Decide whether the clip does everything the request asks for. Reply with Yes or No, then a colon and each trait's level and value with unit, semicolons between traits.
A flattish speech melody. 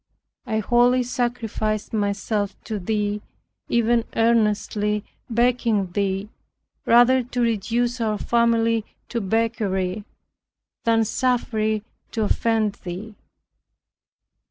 Yes: narrow, 2.2 semitones